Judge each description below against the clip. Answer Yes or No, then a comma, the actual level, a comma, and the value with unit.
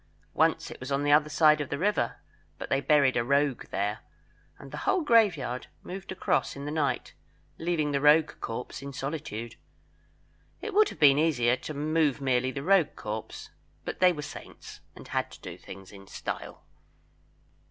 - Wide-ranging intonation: No, average, 3.7 semitones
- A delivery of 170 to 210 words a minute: Yes, average, 180 wpm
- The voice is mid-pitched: Yes, medium, 145 Hz